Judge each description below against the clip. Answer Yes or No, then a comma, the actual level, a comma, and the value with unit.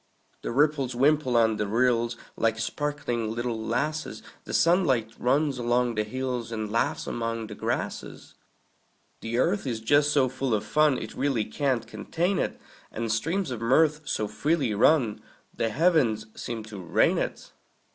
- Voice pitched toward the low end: Yes, low, 125 Hz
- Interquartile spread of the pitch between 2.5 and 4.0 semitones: No, average, 4.5 semitones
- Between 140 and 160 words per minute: Yes, average, 155 wpm